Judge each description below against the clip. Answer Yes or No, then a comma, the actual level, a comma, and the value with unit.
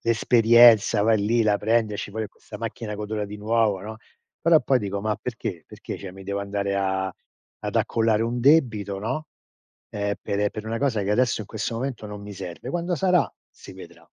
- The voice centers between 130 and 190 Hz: No, low, 110 Hz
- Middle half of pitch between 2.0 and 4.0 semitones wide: Yes, narrow, 2.4 semitones